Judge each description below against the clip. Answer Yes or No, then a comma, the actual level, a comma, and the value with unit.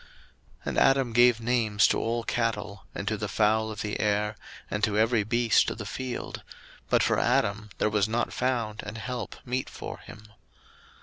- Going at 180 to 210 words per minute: Yes, average, 185 wpm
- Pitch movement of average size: No, narrow, 2.3 semitones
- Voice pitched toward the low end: Yes, low, 110 Hz